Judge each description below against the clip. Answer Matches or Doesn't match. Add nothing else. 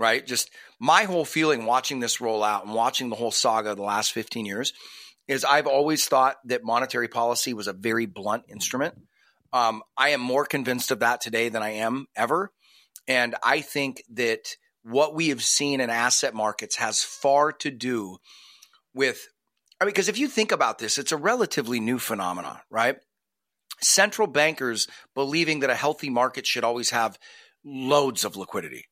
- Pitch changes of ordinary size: Matches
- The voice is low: Matches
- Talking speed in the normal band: Matches